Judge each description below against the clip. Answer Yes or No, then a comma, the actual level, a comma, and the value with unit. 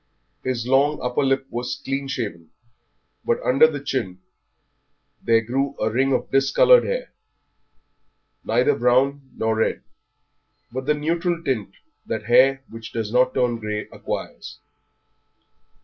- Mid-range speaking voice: No, low, 130 Hz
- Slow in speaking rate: Yes, slow, 130 wpm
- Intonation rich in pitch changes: No, average, 3.2 semitones